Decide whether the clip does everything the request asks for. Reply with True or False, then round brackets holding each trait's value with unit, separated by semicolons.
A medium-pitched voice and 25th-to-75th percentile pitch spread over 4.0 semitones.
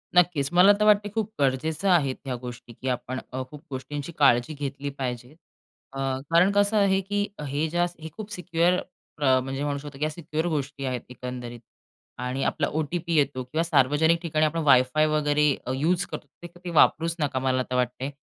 True (150 Hz; 4.6 semitones)